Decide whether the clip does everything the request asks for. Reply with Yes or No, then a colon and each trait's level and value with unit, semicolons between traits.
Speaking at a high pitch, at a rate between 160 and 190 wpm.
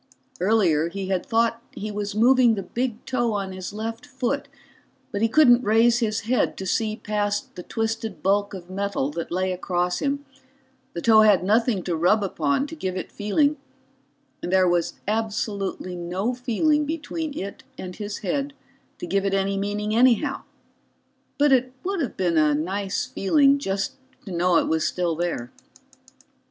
Yes: high, 205 Hz; average, 170 wpm